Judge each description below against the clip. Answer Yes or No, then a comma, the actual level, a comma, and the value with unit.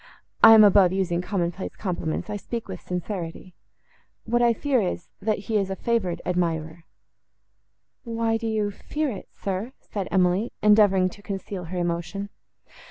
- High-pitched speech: Yes, high, 195 Hz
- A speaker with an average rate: Yes, average, 155 wpm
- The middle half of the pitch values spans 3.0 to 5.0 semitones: Yes, average, 3.5 semitones